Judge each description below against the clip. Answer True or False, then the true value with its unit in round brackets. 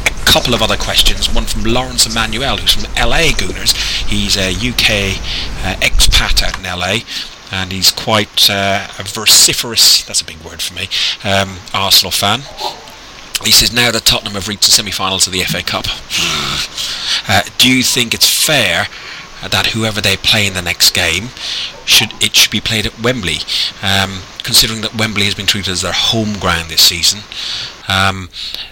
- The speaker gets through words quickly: False (170 wpm)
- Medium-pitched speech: False (100 Hz)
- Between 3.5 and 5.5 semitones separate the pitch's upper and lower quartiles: False (3.1 semitones)